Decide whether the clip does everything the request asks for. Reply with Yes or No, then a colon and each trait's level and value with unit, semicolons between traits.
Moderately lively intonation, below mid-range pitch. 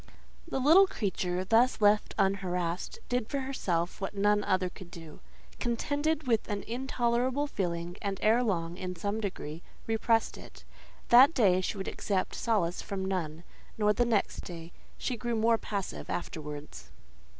No: average, 4.7 semitones; high, 205 Hz